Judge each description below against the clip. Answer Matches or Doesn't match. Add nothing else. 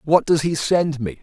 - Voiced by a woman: Doesn't match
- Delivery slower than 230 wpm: Doesn't match